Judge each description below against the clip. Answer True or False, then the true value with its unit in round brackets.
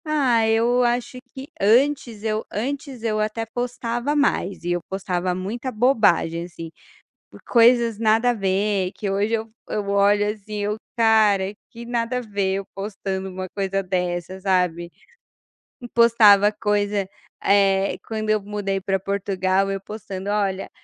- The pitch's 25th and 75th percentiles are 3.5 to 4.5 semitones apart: False (3.0 semitones)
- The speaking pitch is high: True (205 Hz)